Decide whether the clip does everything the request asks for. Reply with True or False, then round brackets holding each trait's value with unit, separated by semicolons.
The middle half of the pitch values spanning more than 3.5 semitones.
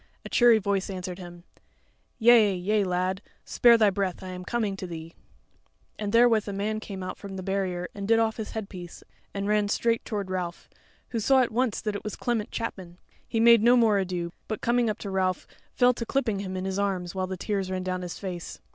False (3.2 semitones)